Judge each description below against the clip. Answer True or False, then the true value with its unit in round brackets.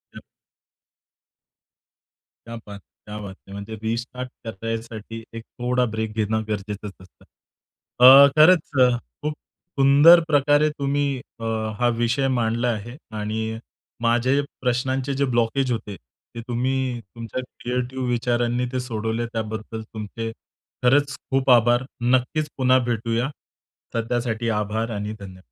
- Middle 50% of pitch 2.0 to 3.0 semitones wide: True (2.7 semitones)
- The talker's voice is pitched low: True (120 Hz)